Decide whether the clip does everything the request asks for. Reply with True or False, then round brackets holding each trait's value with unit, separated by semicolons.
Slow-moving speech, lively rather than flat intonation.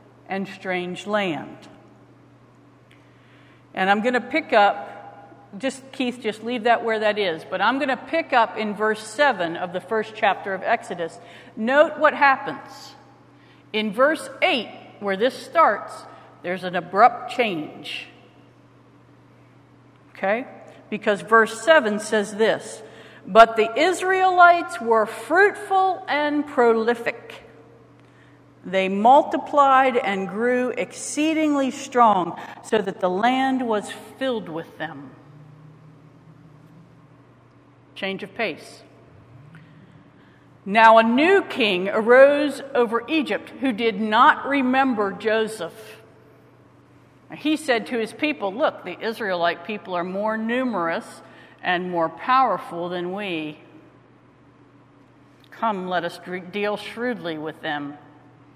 True (115 wpm; 6.9 semitones)